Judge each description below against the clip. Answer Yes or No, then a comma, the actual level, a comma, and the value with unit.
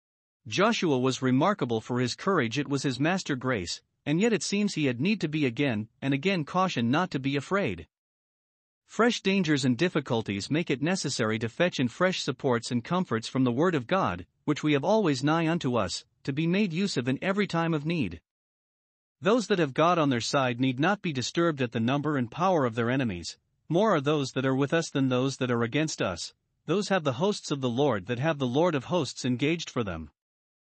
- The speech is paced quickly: Yes, fast, 220 wpm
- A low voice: No, medium, 145 Hz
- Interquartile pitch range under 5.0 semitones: No, average, 5.3 semitones